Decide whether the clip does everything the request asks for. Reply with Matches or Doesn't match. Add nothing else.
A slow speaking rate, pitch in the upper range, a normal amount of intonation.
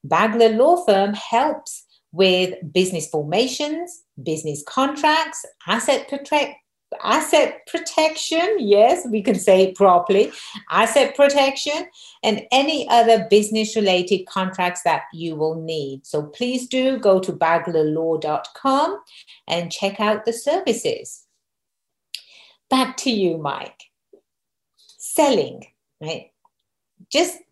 Doesn't match